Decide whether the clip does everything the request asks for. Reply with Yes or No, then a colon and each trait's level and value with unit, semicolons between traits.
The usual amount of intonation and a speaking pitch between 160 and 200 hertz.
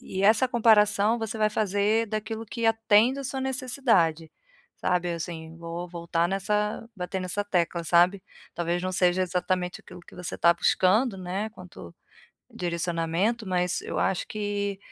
Yes: average, 3.6 semitones; high, 190 Hz